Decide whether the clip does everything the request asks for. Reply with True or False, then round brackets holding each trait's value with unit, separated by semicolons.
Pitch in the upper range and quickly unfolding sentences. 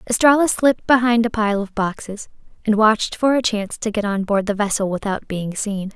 True (215 Hz; 210 wpm)